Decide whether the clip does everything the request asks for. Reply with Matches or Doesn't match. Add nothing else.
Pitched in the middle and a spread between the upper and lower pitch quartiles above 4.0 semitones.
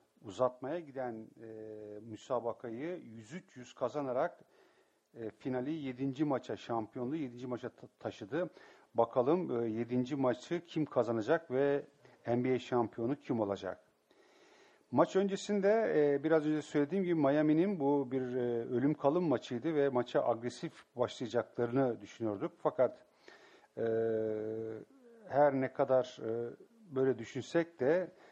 Doesn't match